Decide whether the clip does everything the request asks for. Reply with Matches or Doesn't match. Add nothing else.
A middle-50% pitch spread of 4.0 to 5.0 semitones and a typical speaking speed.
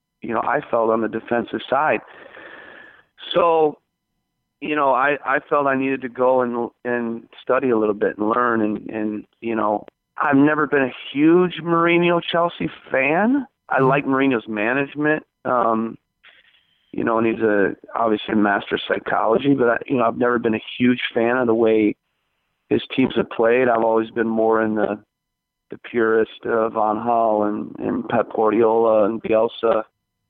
Doesn't match